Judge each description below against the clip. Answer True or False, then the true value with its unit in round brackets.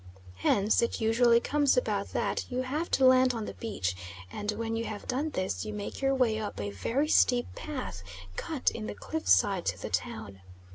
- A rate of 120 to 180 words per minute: False (195 wpm)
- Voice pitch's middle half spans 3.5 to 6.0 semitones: True (4.1 semitones)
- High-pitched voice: True (230 Hz)